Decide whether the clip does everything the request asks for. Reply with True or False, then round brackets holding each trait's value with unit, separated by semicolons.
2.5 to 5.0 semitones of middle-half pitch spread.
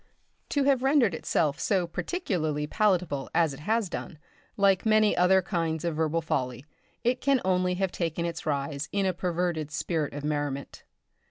True (4.4 semitones)